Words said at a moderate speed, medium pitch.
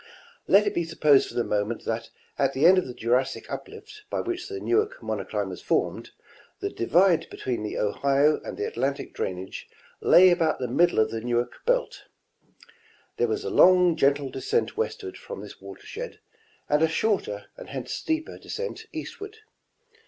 Yes: average, 175 wpm; medium, 170 Hz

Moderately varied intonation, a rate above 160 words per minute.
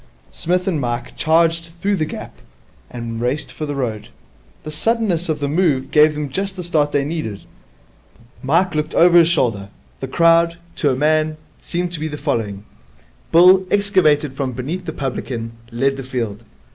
Yes: average, 4.4 semitones; average, 170 wpm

